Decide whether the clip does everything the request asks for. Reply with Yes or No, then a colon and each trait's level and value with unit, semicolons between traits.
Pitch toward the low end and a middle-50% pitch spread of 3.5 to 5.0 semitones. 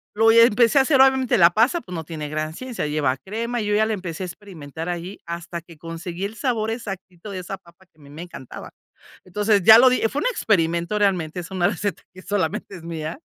No: medium, 185 Hz; average, 4.7 semitones